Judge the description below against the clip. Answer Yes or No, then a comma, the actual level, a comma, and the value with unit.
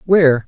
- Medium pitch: Yes, medium, 155 Hz